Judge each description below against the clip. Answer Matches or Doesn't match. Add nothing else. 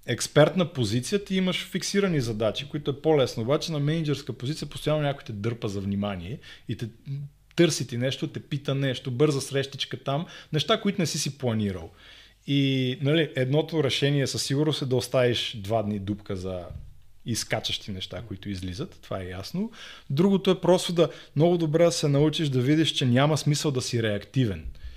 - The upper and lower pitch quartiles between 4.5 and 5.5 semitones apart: Matches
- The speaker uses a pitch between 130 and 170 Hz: Matches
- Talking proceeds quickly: Matches